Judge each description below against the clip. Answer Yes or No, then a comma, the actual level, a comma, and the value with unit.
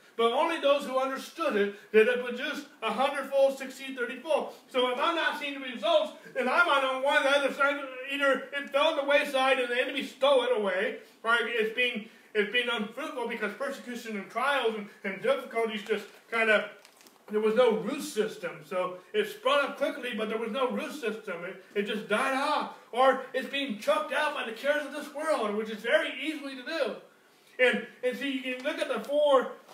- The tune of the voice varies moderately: Yes, average, 4.0 semitones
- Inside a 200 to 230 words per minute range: Yes, fast, 205 wpm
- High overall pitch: Yes, very high, 260 Hz